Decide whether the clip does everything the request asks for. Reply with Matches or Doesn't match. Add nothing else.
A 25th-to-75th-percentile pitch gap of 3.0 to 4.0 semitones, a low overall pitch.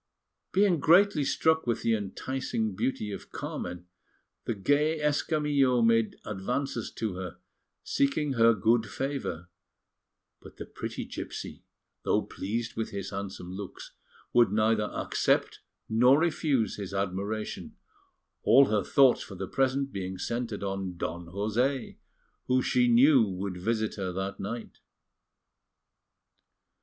Doesn't match